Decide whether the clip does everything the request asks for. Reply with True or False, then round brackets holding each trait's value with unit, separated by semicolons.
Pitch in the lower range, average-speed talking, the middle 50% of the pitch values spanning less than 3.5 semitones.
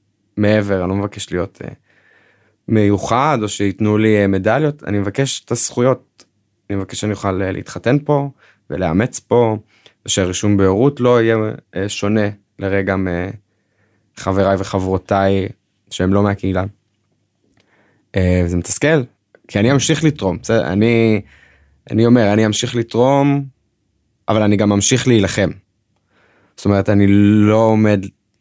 True (105 Hz; 115 wpm; 2.7 semitones)